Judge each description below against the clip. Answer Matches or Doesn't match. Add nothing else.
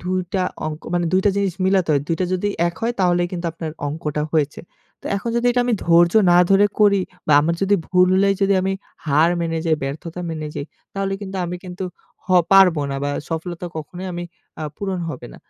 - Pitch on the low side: Doesn't match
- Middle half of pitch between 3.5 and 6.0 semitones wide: Doesn't match